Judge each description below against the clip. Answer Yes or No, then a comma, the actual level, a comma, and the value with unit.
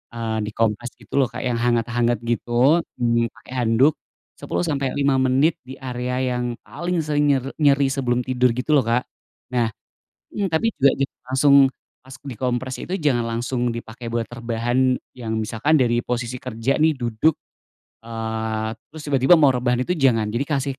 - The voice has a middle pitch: No, low, 125 Hz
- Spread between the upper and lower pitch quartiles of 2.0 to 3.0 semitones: Yes, average, 2.7 semitones